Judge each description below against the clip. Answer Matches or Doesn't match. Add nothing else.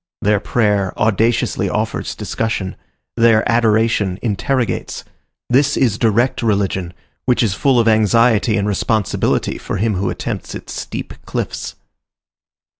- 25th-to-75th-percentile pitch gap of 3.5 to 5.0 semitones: Doesn't match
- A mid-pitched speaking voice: Doesn't match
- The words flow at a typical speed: Doesn't match